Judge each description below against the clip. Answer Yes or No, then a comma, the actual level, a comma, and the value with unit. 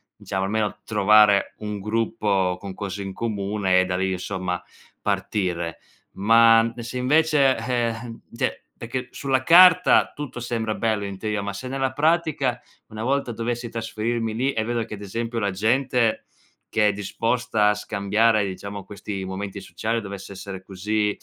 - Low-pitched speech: Yes, low, 110 Hz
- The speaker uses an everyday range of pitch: Yes, average, 3.1 semitones